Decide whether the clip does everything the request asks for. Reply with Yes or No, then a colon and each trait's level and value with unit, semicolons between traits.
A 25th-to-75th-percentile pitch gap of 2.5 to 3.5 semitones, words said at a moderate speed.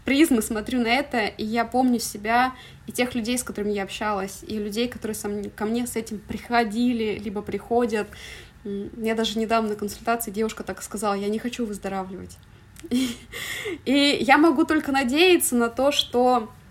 No: average, 2.9 semitones; fast, 170 wpm